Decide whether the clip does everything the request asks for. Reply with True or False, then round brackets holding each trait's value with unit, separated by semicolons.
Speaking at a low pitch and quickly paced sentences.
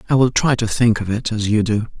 True (115 Hz; 300 wpm)